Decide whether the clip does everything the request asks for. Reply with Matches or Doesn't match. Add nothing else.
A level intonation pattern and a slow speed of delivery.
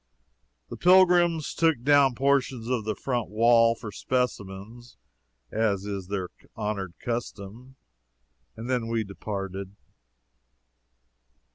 Doesn't match